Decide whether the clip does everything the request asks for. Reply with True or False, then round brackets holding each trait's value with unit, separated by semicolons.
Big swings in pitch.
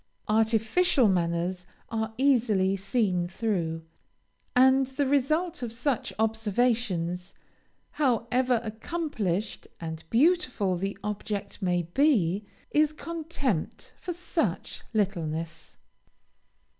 True (6.0 semitones)